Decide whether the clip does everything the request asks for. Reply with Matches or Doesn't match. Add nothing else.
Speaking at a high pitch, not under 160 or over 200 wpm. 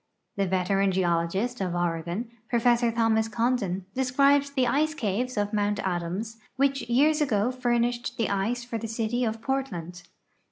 Doesn't match